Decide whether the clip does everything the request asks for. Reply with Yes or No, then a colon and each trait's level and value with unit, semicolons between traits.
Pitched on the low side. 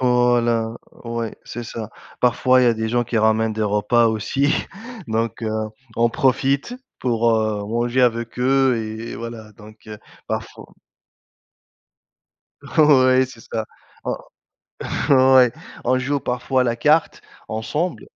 Yes: low, 120 Hz